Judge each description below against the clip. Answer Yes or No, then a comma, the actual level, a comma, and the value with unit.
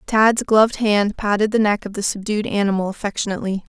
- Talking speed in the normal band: Yes, average, 175 wpm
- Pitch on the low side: No, high, 205 Hz